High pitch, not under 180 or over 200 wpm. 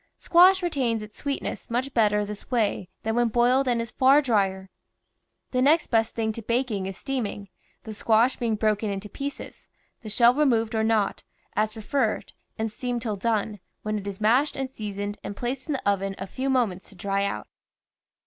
Yes: high, 225 Hz; average, 190 wpm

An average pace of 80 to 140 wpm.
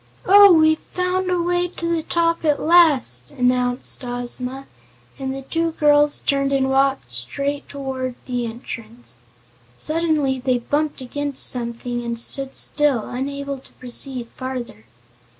Yes: slow, 135 wpm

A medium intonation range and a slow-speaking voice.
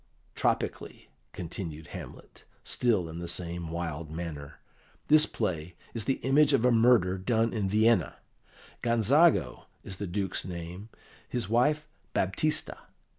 No: wide, 5.8 semitones; slow, 125 wpm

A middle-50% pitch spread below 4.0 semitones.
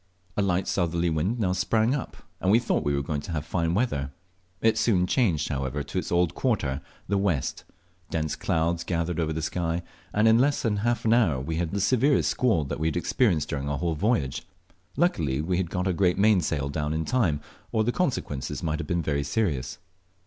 No: wide, 5.6 semitones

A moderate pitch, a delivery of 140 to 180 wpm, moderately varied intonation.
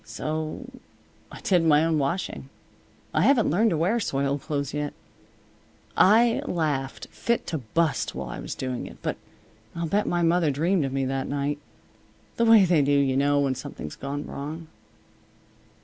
Yes: medium, 155 Hz; average, 165 wpm; average, 3.9 semitones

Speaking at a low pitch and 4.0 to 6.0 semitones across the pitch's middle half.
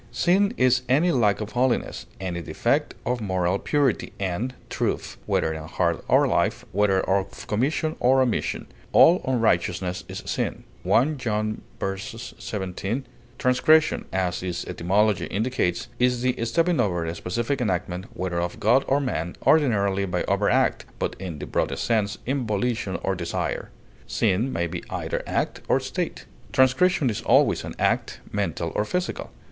Yes: low, 110 Hz; wide, 5.6 semitones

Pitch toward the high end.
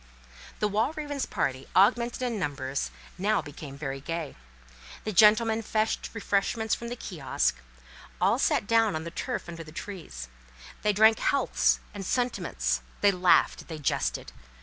Yes: high, 200 Hz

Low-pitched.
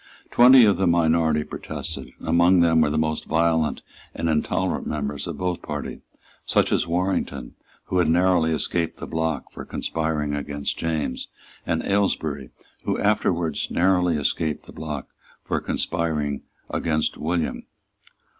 Yes: very low, 80 Hz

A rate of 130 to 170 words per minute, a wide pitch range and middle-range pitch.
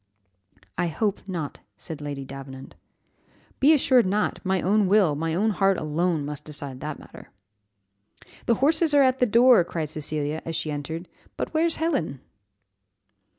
Yes: average, 150 wpm; wide, 6.7 semitones; medium, 170 Hz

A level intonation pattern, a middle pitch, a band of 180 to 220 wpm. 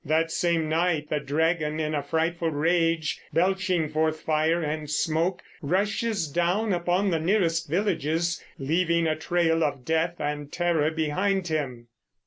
No: narrow, 2.2 semitones; medium, 165 Hz; average, 140 wpm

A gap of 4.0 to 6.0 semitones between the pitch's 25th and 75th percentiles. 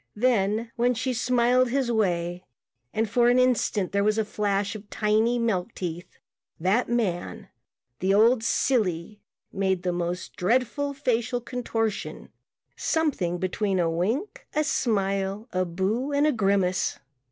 Yes: average, 4.4 semitones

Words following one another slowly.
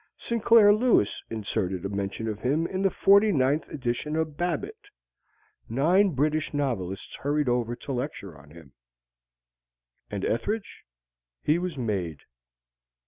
Yes: slow, 130 wpm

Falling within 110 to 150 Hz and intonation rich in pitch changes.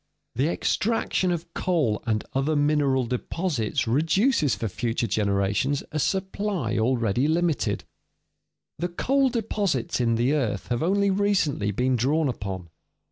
Yes: medium, 140 Hz; wide, 7.4 semitones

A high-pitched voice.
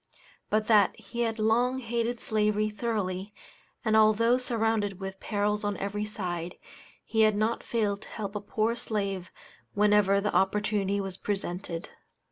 Yes: high, 210 Hz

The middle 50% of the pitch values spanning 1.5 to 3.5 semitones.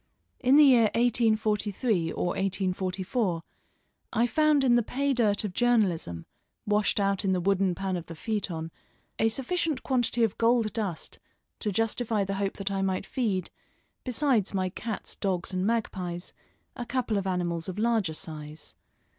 No: average, 4.1 semitones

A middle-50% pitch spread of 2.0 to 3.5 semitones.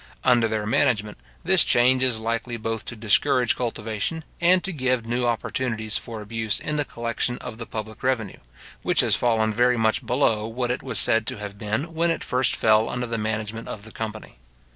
Yes: narrow, 2.5 semitones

